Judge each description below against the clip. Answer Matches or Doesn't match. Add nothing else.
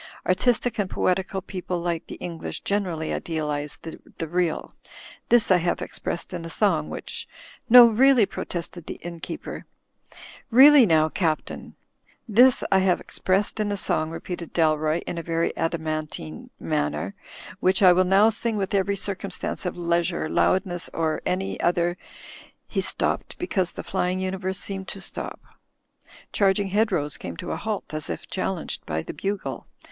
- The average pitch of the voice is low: Doesn't match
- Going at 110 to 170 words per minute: Matches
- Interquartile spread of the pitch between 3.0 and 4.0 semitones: Matches